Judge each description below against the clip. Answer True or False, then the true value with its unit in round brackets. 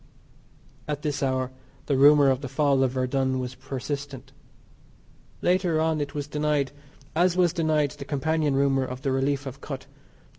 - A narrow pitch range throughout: True (2.1 semitones)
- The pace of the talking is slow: False (160 wpm)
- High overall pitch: False (140 Hz)